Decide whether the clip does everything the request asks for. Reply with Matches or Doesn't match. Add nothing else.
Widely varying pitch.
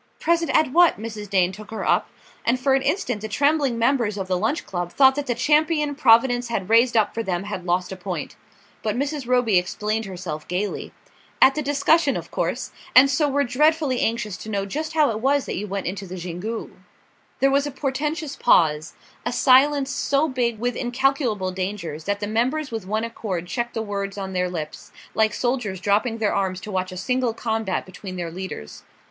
Matches